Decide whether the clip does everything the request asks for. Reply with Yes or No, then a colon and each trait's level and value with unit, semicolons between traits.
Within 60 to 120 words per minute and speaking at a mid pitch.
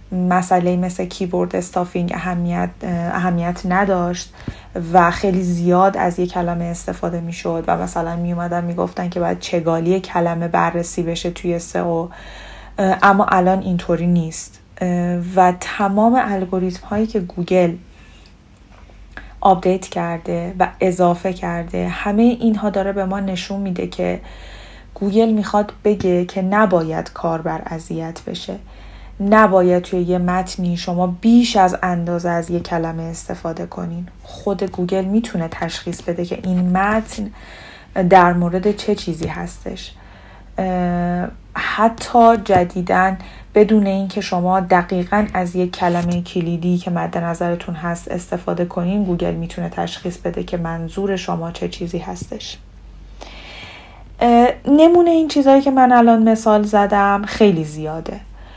No: average, 130 wpm; medium, 180 Hz